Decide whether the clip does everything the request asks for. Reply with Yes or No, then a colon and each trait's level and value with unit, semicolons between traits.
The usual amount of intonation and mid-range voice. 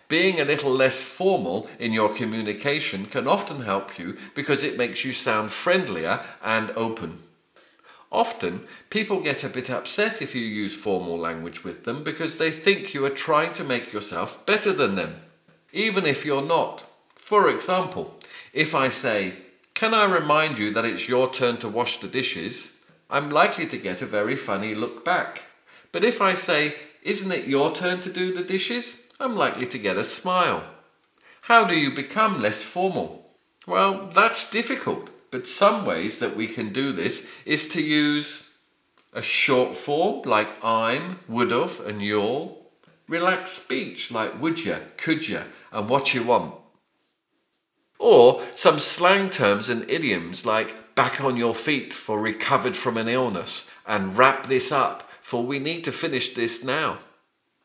No: wide, 7.9 semitones; medium, 145 Hz